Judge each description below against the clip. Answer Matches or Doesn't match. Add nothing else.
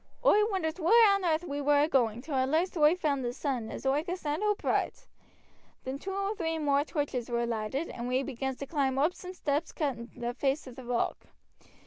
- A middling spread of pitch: Matches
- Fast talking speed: Matches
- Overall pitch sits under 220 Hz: Doesn't match